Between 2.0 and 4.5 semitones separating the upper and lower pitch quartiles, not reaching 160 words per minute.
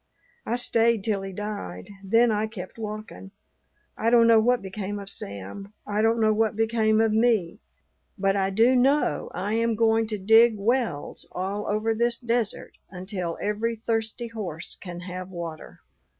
No: average, 2.8 semitones; average, 165 wpm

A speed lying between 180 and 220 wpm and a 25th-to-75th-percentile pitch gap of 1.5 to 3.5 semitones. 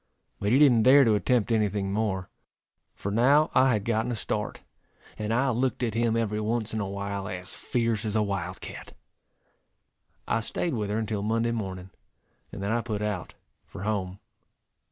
Yes: average, 185 wpm; narrow, 2.6 semitones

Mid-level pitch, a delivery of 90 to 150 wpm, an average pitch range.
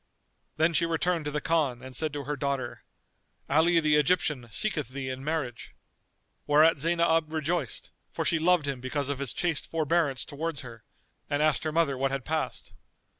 No: medium, 150 Hz; average, 175 wpm; average, 3.2 semitones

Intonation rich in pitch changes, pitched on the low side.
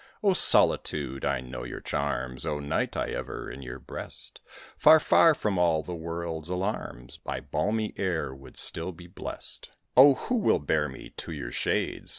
Yes: wide, 6.6 semitones; very low, 85 Hz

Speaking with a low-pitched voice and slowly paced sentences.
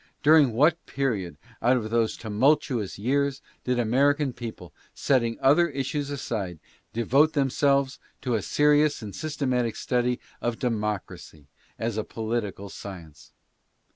Yes: low, 125 Hz; slow, 130 wpm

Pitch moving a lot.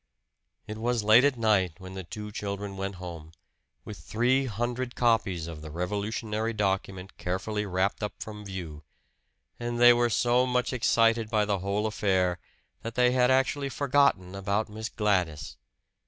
No: average, 4.0 semitones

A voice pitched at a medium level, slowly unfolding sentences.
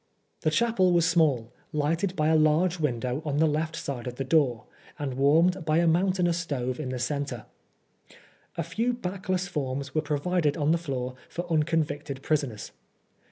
No: medium, 155 Hz; average, 170 wpm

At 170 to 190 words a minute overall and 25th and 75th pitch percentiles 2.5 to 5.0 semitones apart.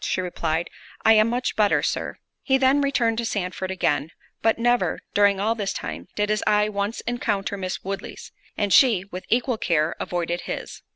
Yes: average, 180 wpm; average, 3.8 semitones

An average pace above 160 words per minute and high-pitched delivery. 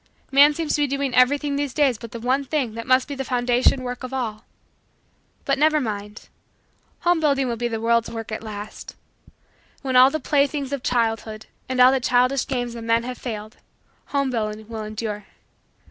Yes: average, 190 wpm; very high, 250 Hz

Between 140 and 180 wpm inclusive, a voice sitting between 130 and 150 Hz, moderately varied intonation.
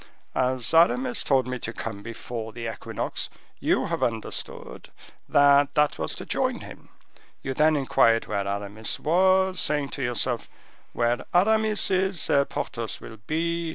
No: average, 150 wpm; low, 135 Hz; wide, 6.4 semitones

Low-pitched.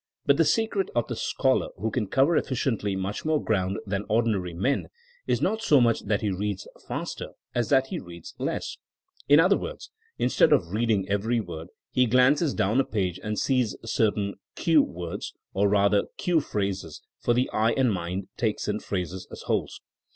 Yes: low, 110 Hz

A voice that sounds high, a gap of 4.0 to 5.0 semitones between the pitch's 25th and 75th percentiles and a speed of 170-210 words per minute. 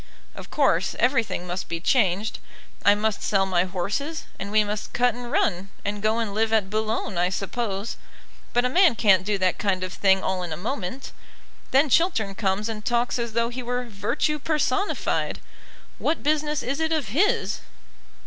Yes: high, 220 Hz; average, 4.5 semitones; average, 180 wpm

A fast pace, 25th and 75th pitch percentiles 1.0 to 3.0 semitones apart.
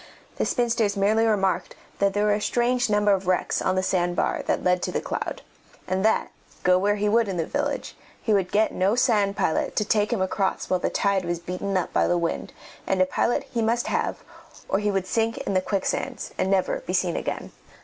Yes: fast, 225 wpm; average, 2.7 semitones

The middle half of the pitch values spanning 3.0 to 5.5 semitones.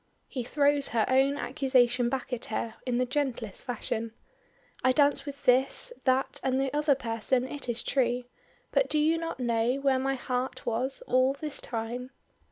No: narrow, 2.4 semitones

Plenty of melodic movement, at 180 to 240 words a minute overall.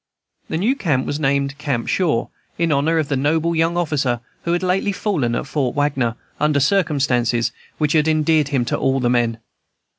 No: average, 3.6 semitones; average, 185 wpm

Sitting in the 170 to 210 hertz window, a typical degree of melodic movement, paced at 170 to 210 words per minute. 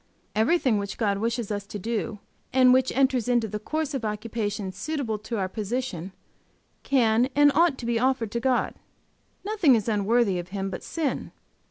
No: high, 230 Hz; average, 3.9 semitones; average, 175 wpm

